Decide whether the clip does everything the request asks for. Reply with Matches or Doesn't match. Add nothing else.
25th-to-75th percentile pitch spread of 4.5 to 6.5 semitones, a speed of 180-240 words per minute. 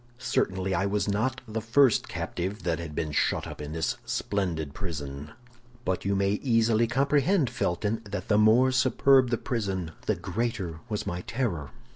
Doesn't match